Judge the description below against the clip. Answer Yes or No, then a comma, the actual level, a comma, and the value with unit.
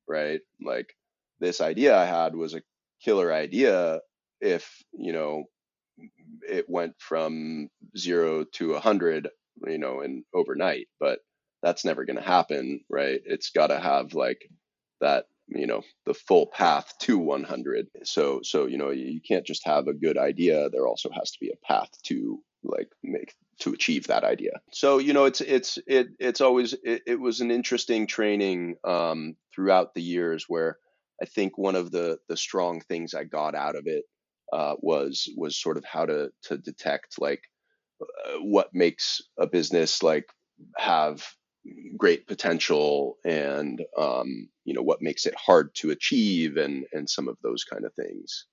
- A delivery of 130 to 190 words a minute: Yes, average, 170 wpm